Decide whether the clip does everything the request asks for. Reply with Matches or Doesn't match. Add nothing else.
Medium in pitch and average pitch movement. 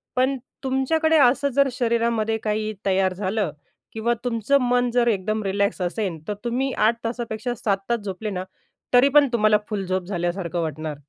Doesn't match